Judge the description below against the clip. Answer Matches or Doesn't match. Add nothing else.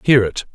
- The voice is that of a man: Matches